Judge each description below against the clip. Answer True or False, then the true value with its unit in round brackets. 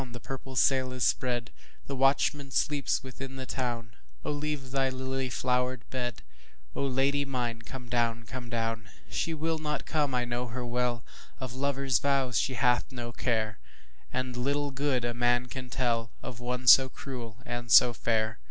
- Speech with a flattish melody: True (2.0 semitones)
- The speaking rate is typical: True (150 wpm)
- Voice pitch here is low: True (125 Hz)